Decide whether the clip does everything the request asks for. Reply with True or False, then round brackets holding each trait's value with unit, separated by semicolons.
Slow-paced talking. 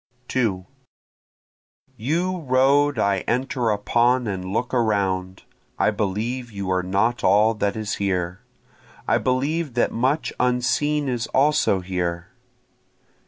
True (120 wpm)